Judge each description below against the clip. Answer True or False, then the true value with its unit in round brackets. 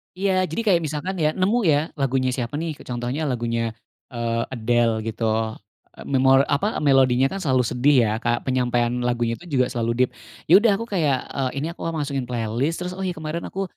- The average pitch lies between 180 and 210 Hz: False (135 Hz)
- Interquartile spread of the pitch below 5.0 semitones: False (5.5 semitones)